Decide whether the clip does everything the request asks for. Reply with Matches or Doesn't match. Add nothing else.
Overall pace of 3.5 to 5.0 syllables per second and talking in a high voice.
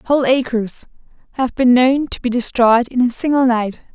Matches